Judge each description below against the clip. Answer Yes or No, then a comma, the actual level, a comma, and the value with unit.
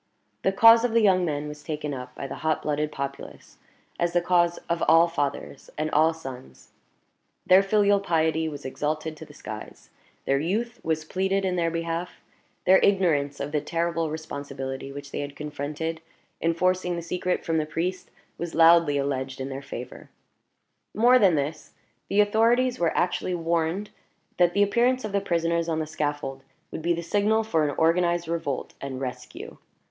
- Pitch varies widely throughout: No, average, 3.8 semitones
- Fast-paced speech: No, average, 175 wpm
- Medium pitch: Yes, medium, 165 Hz